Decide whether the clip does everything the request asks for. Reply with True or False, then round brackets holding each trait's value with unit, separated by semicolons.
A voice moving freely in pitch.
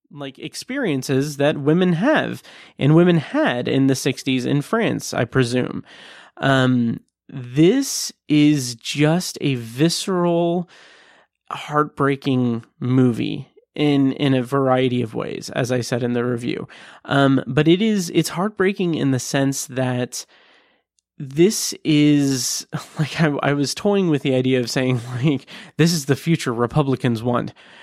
False (4.1 semitones)